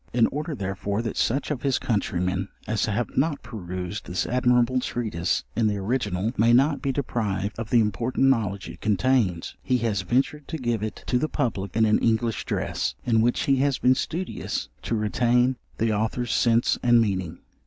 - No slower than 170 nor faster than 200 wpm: Yes, average, 185 wpm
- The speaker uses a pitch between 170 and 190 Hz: No, low, 115 Hz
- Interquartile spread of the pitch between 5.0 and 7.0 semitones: No, average, 3.6 semitones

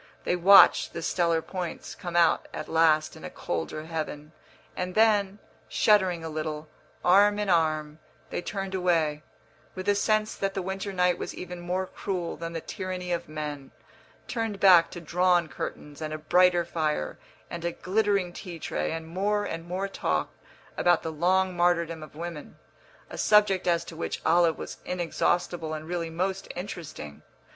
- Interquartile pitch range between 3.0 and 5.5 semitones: No, narrow, 2.6 semitones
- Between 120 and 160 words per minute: No, average, 170 wpm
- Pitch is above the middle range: No, medium, 175 Hz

